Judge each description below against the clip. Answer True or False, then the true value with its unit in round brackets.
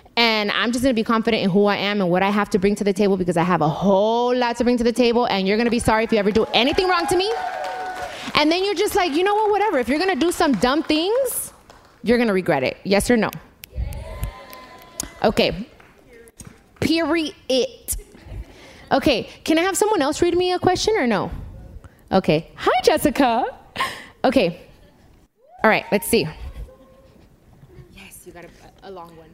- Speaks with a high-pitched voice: True (240 Hz)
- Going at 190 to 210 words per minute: True (195 wpm)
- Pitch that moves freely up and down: True (8.8 semitones)